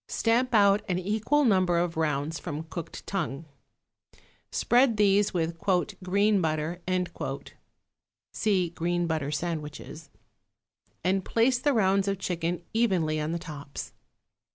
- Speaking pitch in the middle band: Yes, medium, 180 Hz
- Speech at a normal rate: No, slow, 120 wpm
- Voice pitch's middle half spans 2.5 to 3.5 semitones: No, average, 4.0 semitones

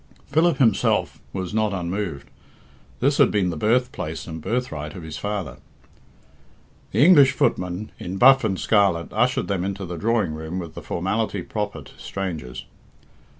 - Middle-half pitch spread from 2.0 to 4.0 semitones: No, wide, 5.6 semitones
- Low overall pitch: Yes, very low, 95 Hz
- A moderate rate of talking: Yes, average, 150 wpm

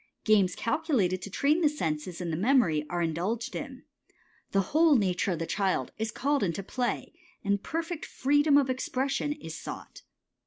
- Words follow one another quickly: No, average, 165 wpm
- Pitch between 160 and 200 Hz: No, high, 215 Hz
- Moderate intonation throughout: No, wide, 7.8 semitones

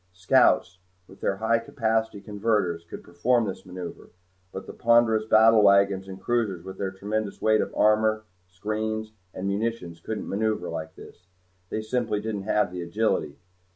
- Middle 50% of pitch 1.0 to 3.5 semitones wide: Yes, narrow, 2.6 semitones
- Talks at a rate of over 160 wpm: No, average, 155 wpm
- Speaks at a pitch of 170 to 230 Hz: No, low, 105 Hz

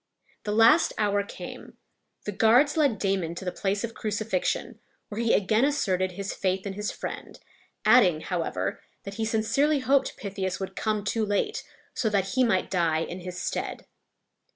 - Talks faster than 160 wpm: Yes, average, 170 wpm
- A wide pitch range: No, average, 3.1 semitones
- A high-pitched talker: Yes, high, 205 Hz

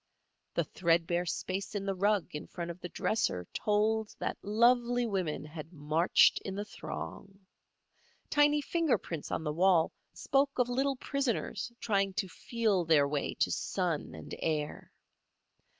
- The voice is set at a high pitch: Yes, high, 195 Hz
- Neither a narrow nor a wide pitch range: No, wide, 6.0 semitones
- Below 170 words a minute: Yes, average, 150 wpm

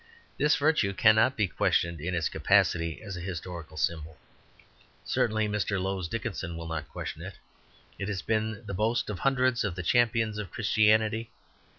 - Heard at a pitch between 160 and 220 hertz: No, low, 105 Hz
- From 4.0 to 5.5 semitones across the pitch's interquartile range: Yes, average, 4.4 semitones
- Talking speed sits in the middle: Yes, average, 165 wpm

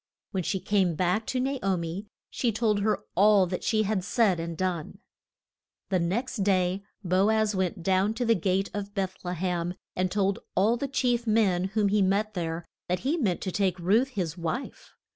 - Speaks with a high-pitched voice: Yes, high, 195 Hz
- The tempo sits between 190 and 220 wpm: Yes, average, 200 wpm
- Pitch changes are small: No, average, 3.1 semitones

